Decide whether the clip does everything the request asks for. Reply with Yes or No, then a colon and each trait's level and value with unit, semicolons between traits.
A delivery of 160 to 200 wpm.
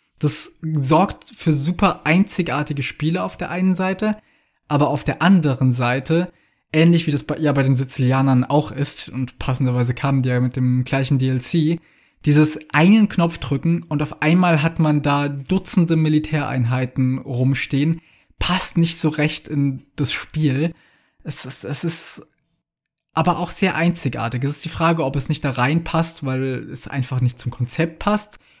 Yes: average, 165 wpm